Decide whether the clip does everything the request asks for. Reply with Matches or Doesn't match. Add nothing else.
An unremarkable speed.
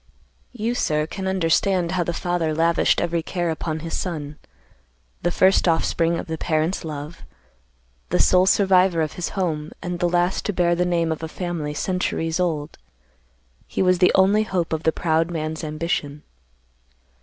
Matches